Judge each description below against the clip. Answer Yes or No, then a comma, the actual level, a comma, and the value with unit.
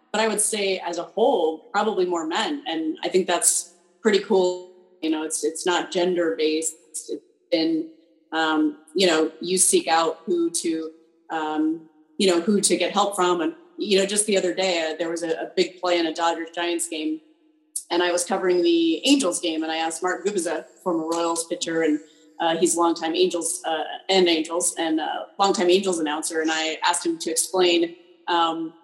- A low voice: No, medium, 175 Hz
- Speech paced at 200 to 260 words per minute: Yes, fast, 205 wpm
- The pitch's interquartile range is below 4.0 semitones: Yes, narrow, 2.5 semitones